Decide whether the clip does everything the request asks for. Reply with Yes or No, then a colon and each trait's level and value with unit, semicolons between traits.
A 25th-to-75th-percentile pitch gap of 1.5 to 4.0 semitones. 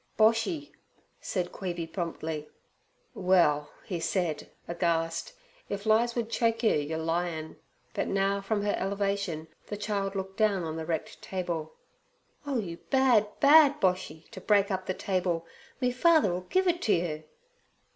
No: average, 4.6 semitones